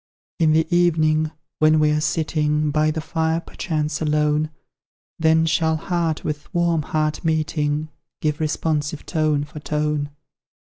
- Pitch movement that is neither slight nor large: No, narrow, 1.0 semitones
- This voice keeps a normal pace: No, slow, 130 wpm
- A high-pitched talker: No, medium, 155 Hz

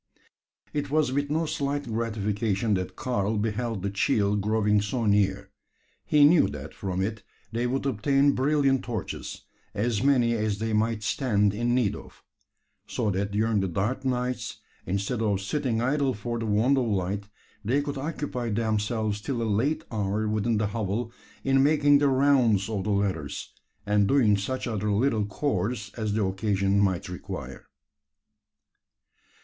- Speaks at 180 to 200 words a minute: No, average, 155 wpm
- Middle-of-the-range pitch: No, low, 110 Hz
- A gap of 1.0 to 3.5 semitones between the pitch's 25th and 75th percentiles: No, average, 4.3 semitones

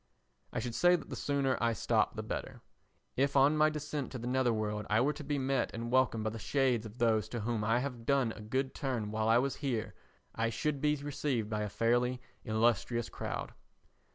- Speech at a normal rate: No, fast, 215 wpm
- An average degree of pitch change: Yes, average, 3.5 semitones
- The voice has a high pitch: No, low, 120 Hz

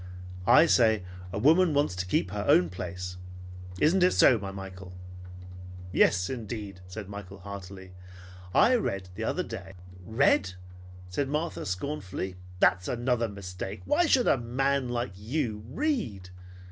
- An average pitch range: No, wide, 6.4 semitones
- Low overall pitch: Yes, low, 105 Hz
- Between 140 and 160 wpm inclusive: Yes, average, 145 wpm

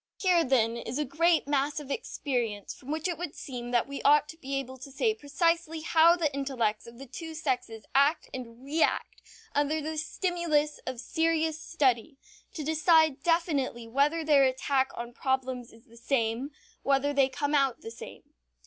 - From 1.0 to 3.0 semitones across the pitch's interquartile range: No, average, 3.7 semitones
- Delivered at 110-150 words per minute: No, average, 175 wpm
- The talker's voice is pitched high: Yes, very high, 280 Hz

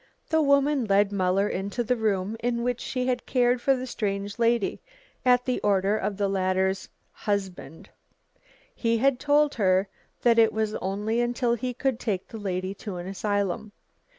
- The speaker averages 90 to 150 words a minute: No, average, 170 wpm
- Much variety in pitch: No, average, 3.9 semitones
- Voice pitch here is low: No, high, 215 Hz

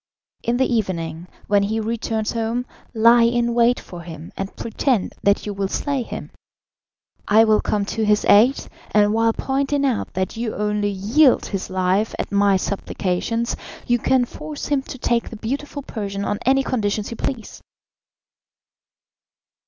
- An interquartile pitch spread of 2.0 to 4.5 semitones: Yes, average, 3.2 semitones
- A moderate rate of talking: Yes, average, 160 wpm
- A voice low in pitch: No, high, 220 Hz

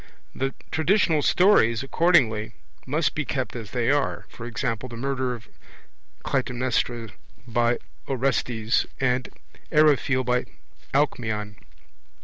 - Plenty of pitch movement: No, average, 3.1 semitones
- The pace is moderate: No, slow, 110 wpm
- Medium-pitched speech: No, low, 125 Hz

